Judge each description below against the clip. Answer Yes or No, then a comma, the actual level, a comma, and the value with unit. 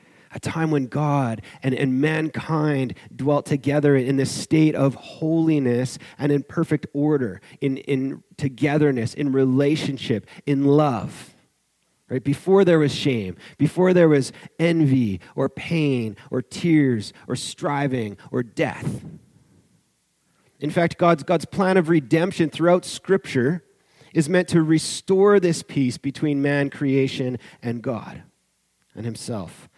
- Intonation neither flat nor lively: Yes, average, 3.6 semitones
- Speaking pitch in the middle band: Yes, medium, 145 Hz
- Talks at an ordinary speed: No, slow, 130 wpm